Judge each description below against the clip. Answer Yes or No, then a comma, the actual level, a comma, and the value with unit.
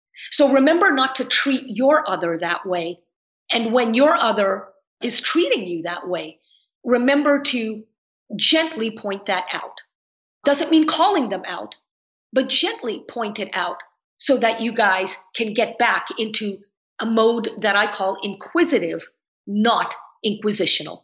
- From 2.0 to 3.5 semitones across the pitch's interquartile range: No, wide, 5.6 semitones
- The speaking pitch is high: Yes, high, 225 Hz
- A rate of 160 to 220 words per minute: No, average, 145 wpm